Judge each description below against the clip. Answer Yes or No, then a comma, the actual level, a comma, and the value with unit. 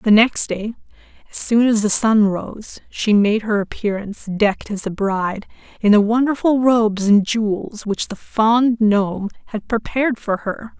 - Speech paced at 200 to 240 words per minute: No, average, 170 wpm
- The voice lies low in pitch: No, high, 215 Hz